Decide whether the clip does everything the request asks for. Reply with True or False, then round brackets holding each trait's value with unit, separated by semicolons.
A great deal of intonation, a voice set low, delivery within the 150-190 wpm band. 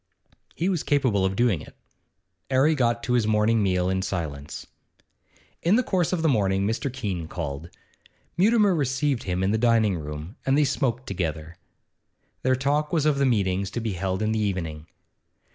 True (6.7 semitones; 110 Hz; 180 wpm)